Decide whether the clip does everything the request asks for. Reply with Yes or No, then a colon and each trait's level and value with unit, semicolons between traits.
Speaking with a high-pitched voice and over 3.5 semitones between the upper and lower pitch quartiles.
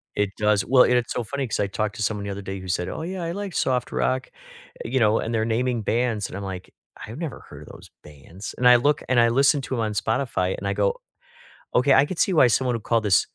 No: low, 115 Hz; average, 4.2 semitones